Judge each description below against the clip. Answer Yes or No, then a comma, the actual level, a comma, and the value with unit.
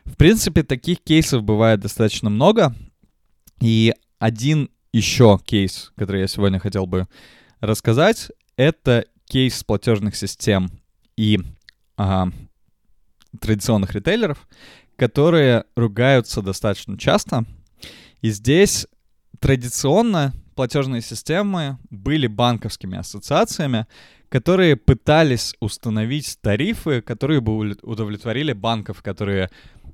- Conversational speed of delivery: No, slow, 90 wpm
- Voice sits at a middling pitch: No, low, 115 Hz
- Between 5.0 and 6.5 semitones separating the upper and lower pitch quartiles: Yes, average, 5.3 semitones